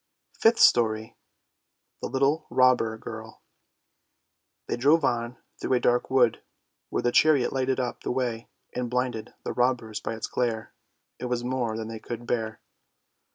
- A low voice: Yes, low, 120 Hz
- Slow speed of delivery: No, average, 155 wpm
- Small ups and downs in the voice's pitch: Yes, narrow, 2.1 semitones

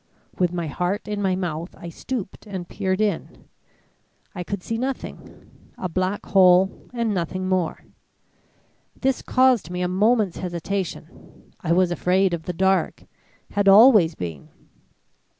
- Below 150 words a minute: Yes, average, 140 wpm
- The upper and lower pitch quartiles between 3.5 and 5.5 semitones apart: No, narrow, 2.5 semitones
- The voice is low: No, medium, 185 Hz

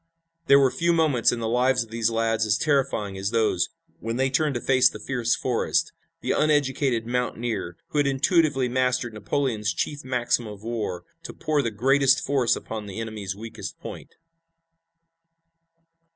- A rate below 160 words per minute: No, average, 165 wpm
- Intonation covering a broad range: No, average, 3.3 semitones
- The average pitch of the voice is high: No, low, 120 Hz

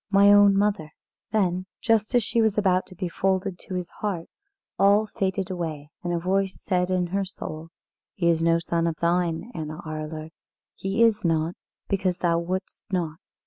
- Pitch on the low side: No, medium, 185 Hz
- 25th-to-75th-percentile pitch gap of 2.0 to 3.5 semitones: Yes, average, 2.9 semitones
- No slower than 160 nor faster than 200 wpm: Yes, average, 180 wpm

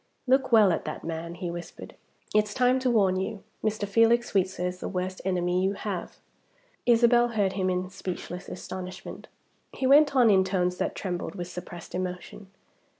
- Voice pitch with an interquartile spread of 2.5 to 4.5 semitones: Yes, average, 3.8 semitones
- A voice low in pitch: No, high, 190 Hz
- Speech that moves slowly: No, average, 170 wpm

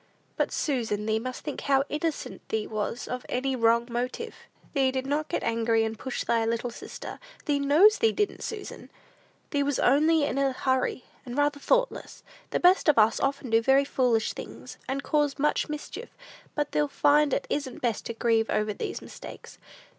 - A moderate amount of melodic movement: Yes, average, 4.1 semitones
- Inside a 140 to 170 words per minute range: No, average, 185 wpm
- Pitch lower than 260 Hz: No, very high, 270 Hz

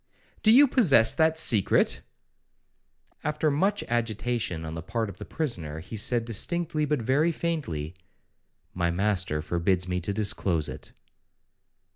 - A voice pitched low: Yes, low, 115 Hz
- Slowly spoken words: Yes, slow, 130 wpm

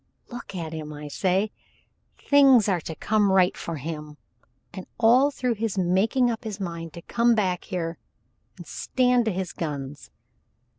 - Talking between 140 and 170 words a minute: Yes, average, 160 wpm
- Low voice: No, high, 190 Hz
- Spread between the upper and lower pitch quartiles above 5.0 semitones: Yes, wide, 5.5 semitones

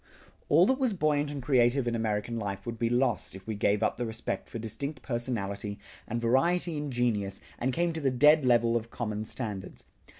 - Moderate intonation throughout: Yes, average, 4.5 semitones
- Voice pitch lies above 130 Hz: No, low, 120 Hz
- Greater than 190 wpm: Yes, average, 200 wpm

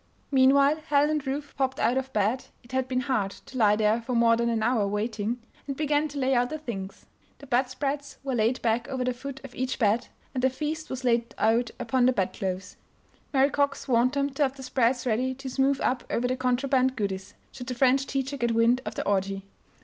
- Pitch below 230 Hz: No, very high, 255 Hz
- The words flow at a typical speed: No, fast, 225 wpm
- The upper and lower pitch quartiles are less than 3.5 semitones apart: Yes, average, 2.8 semitones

